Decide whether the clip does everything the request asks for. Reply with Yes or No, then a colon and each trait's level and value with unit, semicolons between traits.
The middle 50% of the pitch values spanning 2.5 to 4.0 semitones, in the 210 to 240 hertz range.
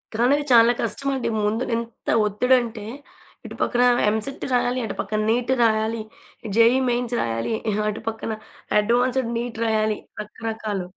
No: narrow, 2.1 semitones; high, 230 Hz